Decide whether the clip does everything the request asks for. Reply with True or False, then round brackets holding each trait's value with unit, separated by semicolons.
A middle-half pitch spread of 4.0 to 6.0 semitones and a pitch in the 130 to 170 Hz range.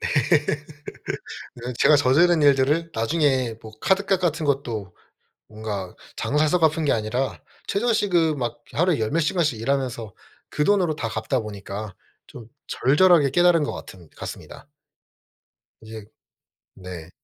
False (7.0 semitones; 140 Hz)